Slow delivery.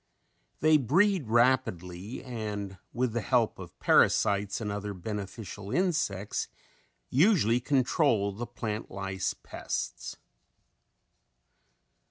Yes: slow, 95 wpm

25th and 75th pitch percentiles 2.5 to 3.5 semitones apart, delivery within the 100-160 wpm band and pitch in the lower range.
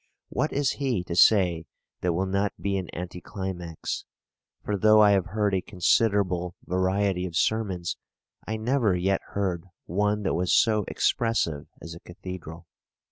Yes: average, 2.9 semitones; average, 155 wpm; very low, 95 Hz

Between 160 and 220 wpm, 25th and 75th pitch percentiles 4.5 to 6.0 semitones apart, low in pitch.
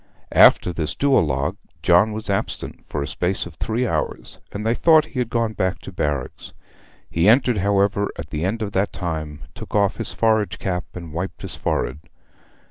Yes: average, 185 wpm; average, 4.9 semitones; very low, 95 Hz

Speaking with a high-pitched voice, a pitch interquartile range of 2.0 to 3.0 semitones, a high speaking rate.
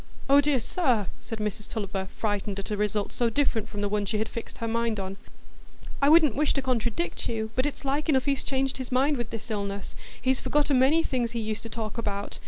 No: high, 230 Hz; average, 4.2 semitones; fast, 225 wpm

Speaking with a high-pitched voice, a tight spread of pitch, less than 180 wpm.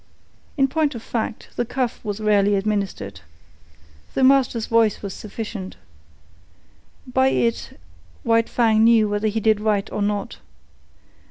Yes: high, 220 Hz; narrow, 2.2 semitones; slow, 135 wpm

